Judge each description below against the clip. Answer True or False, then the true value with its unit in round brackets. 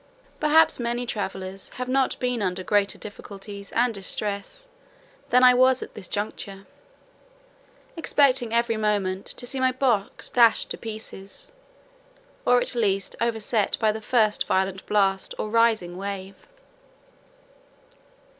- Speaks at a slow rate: True (125 wpm)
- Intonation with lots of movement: False (3.8 semitones)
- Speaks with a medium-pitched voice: False (215 Hz)